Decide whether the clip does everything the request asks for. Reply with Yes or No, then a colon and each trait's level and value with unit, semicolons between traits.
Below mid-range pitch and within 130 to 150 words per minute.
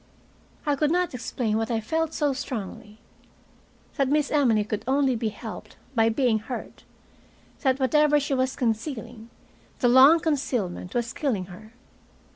No: very high, 250 Hz; average, 145 wpm